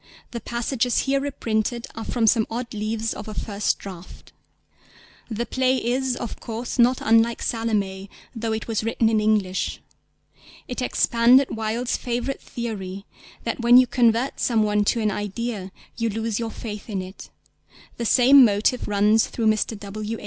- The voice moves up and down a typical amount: No, narrow, 2.2 semitones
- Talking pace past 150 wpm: Yes, average, 160 wpm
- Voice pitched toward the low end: No, high, 225 Hz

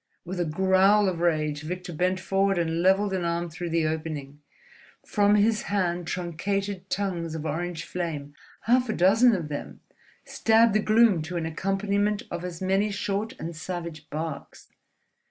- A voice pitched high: No, medium, 180 Hz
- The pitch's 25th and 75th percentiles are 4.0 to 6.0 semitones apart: No, average, 3.4 semitones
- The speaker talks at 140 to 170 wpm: Yes, average, 160 wpm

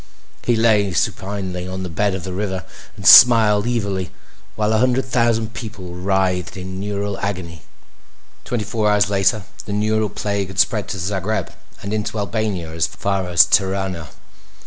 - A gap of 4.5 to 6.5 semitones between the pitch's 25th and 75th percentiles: No, narrow, 2.5 semitones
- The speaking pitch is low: Yes, low, 100 Hz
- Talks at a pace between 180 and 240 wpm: No, average, 160 wpm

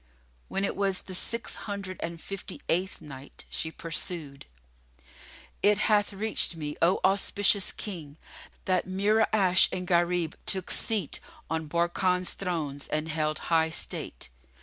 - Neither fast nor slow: No, slow, 130 wpm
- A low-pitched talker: No, medium, 180 Hz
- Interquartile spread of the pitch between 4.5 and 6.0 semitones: No, average, 3.4 semitones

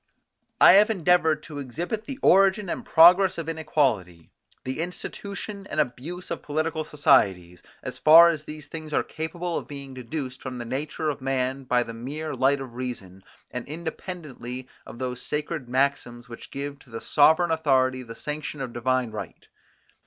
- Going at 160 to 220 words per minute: Yes, average, 165 wpm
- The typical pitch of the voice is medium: Yes, medium, 145 Hz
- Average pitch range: Yes, average, 4.3 semitones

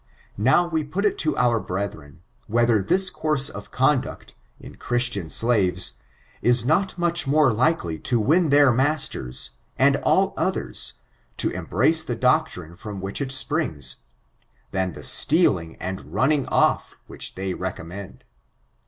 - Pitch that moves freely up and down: Yes, wide, 8.2 semitones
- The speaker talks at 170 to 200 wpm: No, average, 140 wpm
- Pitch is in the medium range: No, low, 120 Hz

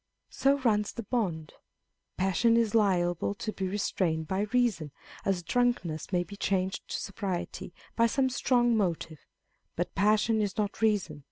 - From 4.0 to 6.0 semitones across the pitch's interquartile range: Yes, average, 4.4 semitones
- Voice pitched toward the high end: Yes, high, 200 Hz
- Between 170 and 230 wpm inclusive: No, average, 160 wpm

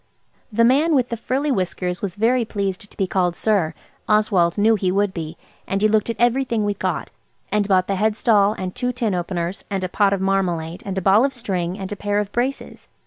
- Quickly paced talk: Yes, fast, 215 wpm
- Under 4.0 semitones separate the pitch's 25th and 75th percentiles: Yes, average, 3.4 semitones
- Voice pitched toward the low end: No, high, 205 Hz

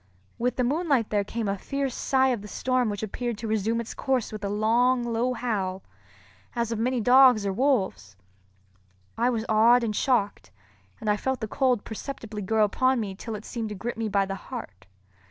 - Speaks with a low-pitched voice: No, high, 225 Hz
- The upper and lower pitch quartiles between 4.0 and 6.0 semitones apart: No, average, 3.2 semitones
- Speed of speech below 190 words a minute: No, average, 200 wpm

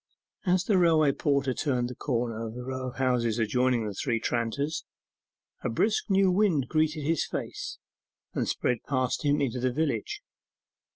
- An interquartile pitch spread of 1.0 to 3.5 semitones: No, average, 4.4 semitones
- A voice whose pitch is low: Yes, low, 130 Hz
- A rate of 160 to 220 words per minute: Yes, average, 165 wpm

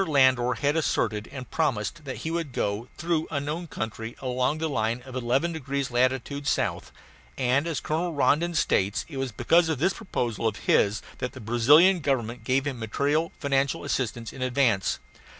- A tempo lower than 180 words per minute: Yes, average, 170 wpm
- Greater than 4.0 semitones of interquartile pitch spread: Yes, average, 4.4 semitones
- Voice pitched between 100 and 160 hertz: Yes, low, 135 Hz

